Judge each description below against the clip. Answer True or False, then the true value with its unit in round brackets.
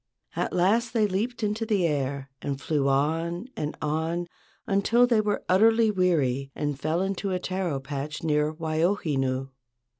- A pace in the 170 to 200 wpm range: False (150 wpm)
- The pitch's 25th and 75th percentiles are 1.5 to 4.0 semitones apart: False (5.6 semitones)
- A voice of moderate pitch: True (170 Hz)